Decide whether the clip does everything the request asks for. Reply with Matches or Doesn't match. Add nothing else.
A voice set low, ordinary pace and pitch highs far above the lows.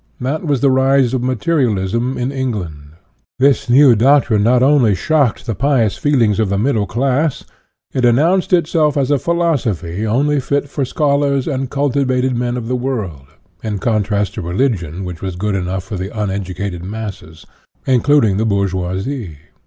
Matches